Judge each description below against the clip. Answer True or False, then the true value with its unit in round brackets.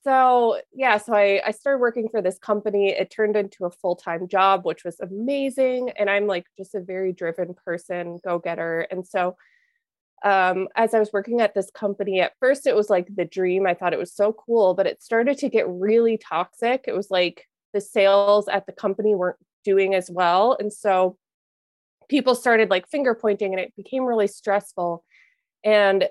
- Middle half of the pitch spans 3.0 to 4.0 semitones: True (3.6 semitones)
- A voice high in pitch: True (200 Hz)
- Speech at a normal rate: True (190 wpm)